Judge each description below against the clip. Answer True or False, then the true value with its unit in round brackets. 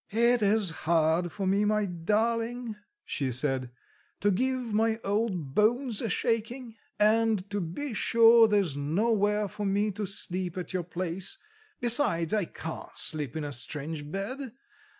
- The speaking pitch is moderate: False (205 Hz)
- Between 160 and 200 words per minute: False (150 wpm)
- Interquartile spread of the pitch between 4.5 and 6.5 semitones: True (5.1 semitones)